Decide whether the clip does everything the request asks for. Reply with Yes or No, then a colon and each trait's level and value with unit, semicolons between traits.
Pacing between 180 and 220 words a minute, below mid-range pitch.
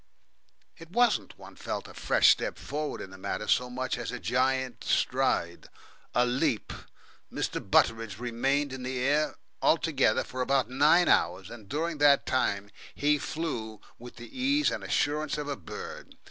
No: average, 160 wpm; low, 130 Hz